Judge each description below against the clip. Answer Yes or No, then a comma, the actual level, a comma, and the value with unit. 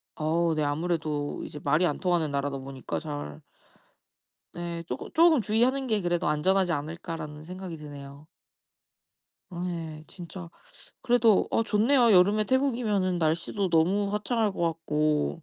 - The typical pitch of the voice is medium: Yes, medium, 170 Hz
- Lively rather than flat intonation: No, average, 5.0 semitones